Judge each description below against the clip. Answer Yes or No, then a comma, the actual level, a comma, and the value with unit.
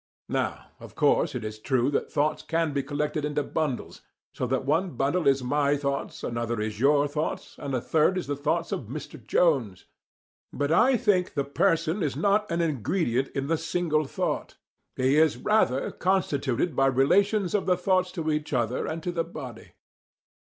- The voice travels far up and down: No, average, 4.0 semitones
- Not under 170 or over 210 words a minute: Yes, average, 180 wpm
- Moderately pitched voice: Yes, medium, 150 Hz